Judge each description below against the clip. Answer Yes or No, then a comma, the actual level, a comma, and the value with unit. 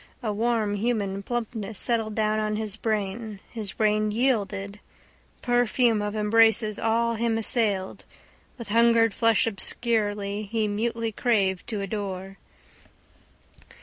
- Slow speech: Yes, slow, 115 wpm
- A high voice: Yes, high, 215 Hz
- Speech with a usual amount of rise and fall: No, narrow, 2.0 semitones